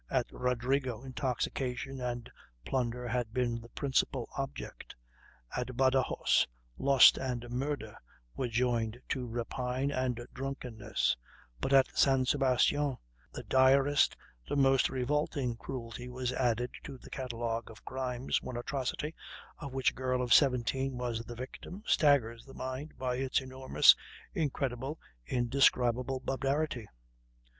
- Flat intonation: Yes, narrow, 1.7 semitones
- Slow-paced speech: Yes, slow, 125 wpm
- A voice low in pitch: Yes, low, 130 Hz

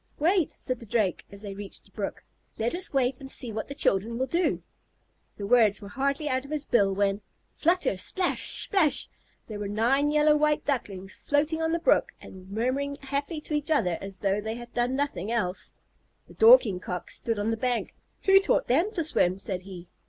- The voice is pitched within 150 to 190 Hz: No, high, 245 Hz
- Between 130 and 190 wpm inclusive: No, fast, 205 wpm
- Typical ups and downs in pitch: No, wide, 6.6 semitones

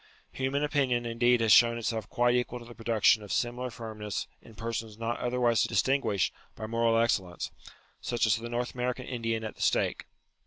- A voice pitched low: Yes, low, 115 Hz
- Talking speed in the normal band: Yes, average, 185 wpm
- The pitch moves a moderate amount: No, narrow, 1.5 semitones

